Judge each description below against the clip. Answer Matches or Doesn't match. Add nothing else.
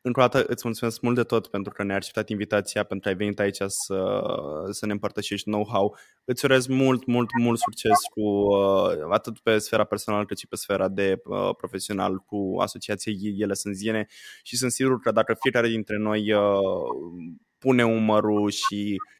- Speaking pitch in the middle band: Doesn't match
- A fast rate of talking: Matches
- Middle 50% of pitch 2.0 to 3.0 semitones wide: Matches